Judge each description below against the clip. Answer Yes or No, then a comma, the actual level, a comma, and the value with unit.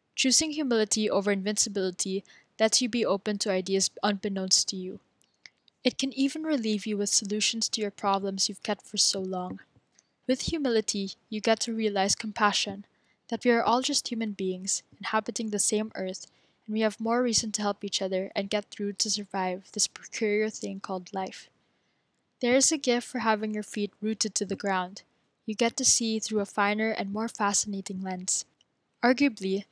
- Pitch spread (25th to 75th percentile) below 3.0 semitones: Yes, narrow, 2.5 semitones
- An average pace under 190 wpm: Yes, average, 180 wpm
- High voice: Yes, high, 210 Hz